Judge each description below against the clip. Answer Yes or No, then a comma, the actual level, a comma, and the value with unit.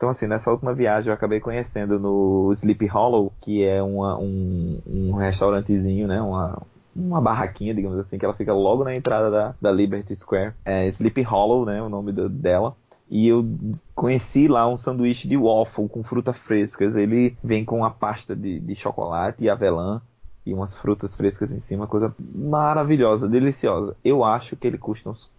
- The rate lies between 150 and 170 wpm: No, average, 180 wpm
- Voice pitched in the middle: No, low, 105 Hz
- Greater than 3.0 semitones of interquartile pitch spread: Yes, average, 3.4 semitones